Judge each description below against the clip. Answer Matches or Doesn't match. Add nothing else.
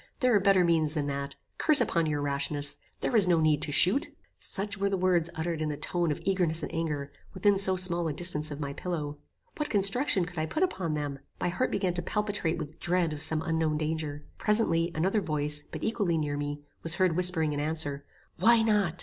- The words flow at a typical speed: Doesn't match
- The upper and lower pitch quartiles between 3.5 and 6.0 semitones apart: Matches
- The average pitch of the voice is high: Doesn't match